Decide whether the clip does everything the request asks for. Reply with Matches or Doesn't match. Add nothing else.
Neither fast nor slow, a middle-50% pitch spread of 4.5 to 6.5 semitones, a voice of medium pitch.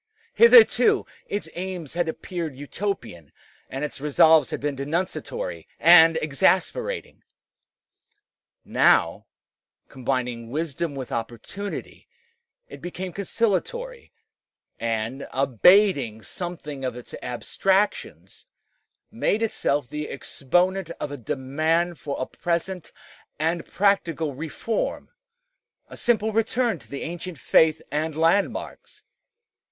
Doesn't match